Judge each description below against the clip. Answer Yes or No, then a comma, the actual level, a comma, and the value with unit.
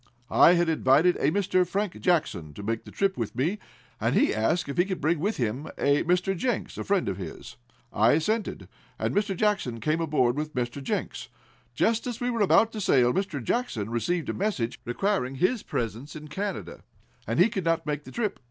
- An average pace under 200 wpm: No, fast, 205 wpm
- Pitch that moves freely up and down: Yes, wide, 7.9 semitones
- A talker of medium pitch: Yes, medium, 165 Hz